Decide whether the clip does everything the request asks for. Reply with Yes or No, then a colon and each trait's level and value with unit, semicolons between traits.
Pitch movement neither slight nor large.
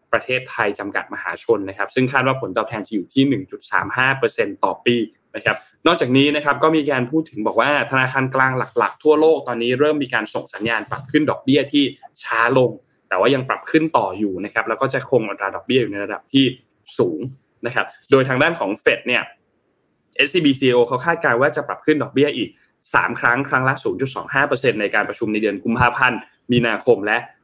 Yes: average, 4.1 semitones